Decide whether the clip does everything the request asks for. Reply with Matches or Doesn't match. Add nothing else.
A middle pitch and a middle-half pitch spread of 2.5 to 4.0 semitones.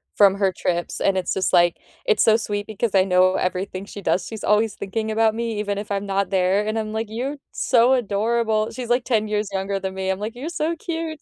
Doesn't match